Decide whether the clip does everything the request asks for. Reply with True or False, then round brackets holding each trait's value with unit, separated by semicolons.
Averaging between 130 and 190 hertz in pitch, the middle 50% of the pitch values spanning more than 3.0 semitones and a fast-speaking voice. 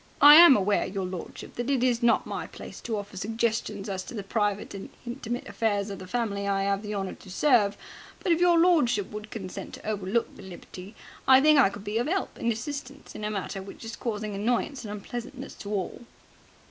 False (215 Hz; 3.5 semitones; 215 wpm)